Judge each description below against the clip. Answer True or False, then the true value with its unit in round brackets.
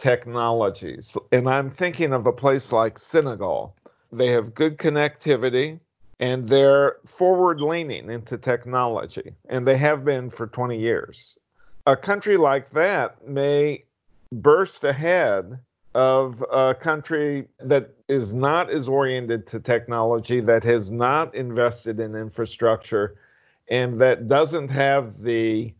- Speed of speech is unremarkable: False (125 wpm)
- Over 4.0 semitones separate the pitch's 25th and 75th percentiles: False (3.4 semitones)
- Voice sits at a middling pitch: False (130 Hz)